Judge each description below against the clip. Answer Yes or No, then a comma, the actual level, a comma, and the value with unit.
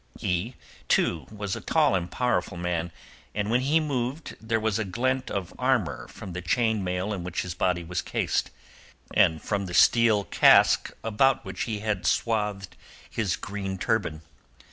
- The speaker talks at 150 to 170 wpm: Yes, average, 165 wpm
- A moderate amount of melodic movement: Yes, average, 4.3 semitones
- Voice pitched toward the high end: No, low, 105 Hz